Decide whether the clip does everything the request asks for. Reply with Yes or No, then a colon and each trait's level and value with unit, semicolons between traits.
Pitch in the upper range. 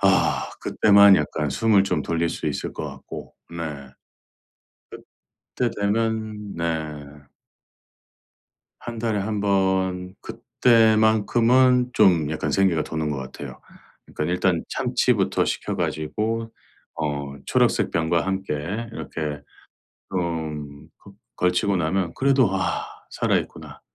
No: very low, 95 Hz